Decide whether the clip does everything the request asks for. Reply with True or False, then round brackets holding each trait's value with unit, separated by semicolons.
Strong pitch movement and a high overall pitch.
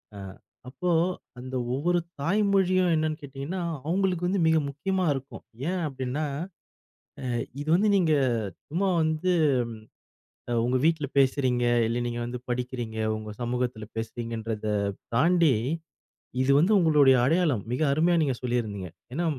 False (6.0 semitones; 140 Hz)